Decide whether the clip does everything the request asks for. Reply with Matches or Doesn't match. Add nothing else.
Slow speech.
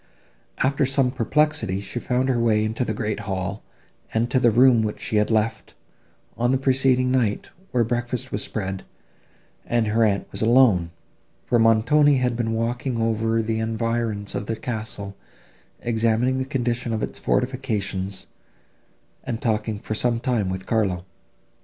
Doesn't match